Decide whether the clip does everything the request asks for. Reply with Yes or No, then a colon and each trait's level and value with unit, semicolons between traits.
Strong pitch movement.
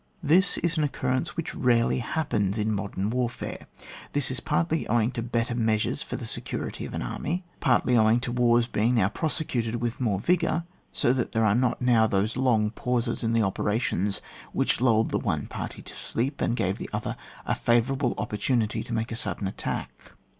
No: average, 2.8 semitones